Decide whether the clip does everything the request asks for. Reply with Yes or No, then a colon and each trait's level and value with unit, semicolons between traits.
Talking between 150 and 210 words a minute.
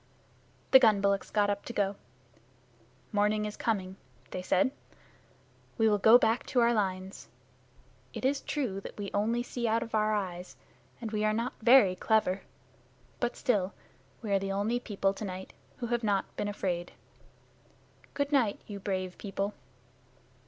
Yes: average, 160 wpm